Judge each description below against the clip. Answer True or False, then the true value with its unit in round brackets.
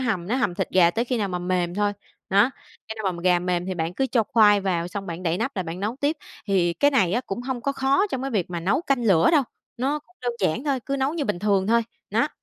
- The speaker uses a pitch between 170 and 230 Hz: True (205 Hz)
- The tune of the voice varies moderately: False (6.5 semitones)